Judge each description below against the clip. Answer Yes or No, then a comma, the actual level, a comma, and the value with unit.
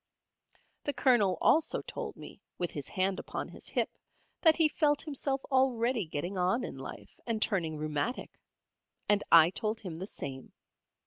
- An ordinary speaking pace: Yes, average, 155 wpm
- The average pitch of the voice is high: Yes, high, 210 Hz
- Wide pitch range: Yes, wide, 7.1 semitones